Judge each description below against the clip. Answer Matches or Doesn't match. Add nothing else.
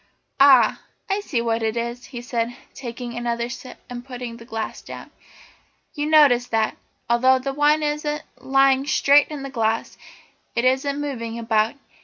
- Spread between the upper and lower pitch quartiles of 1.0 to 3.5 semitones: Matches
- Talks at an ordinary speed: Matches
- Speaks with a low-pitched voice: Doesn't match